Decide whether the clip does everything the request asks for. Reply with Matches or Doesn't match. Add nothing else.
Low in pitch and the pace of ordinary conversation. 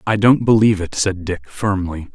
Matches